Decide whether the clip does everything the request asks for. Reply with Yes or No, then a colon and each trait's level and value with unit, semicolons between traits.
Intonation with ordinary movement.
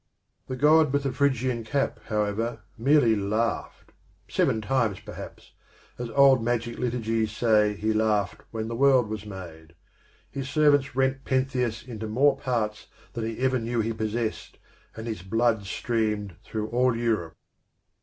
Yes: average, 3.1 semitones